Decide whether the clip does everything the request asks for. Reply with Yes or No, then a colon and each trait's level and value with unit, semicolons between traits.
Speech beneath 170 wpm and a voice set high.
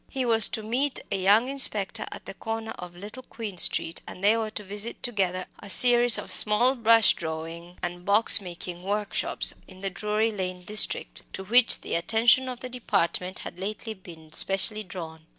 No: average, 185 wpm; high, 205 Hz